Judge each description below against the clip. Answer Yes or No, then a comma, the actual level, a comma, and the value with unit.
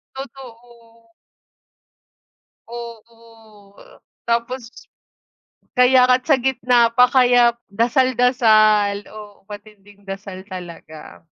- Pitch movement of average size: Yes, average, 3.2 semitones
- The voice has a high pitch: Yes, high, 230 Hz